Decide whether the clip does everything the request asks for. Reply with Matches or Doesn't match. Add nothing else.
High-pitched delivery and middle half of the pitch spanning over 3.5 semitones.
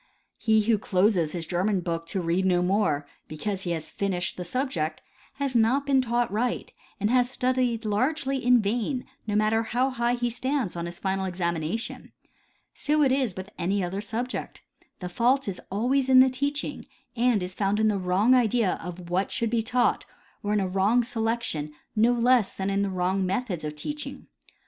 Matches